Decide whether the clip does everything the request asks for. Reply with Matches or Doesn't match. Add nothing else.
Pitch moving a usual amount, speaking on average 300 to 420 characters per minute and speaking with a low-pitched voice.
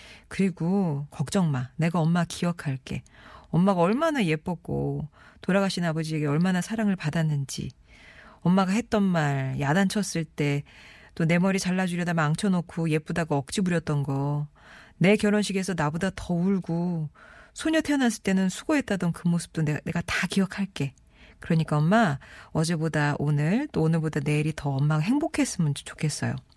Doesn't match